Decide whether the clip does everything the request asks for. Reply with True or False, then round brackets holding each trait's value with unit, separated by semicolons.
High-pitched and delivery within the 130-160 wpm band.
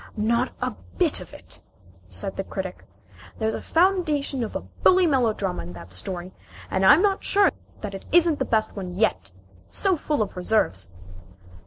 False (220 Hz; 170 wpm)